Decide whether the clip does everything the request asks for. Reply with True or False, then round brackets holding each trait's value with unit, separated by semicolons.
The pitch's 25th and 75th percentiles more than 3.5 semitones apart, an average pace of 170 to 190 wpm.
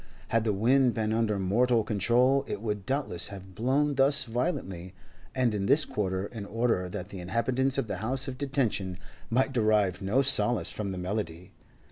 True (4.8 semitones; 175 wpm)